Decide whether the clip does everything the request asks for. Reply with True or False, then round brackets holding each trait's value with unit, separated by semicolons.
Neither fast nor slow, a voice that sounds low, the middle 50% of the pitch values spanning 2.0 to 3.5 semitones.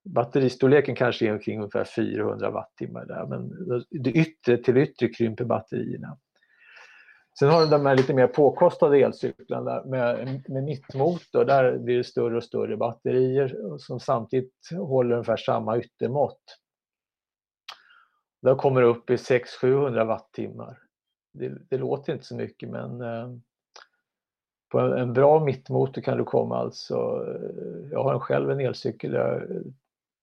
True (135 wpm; 130 Hz; 3.0 semitones)